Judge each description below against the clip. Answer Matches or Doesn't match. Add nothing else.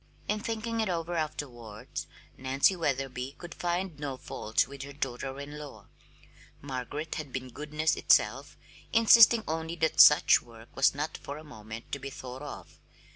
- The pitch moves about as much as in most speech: Matches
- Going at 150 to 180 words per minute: Matches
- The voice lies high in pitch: Doesn't match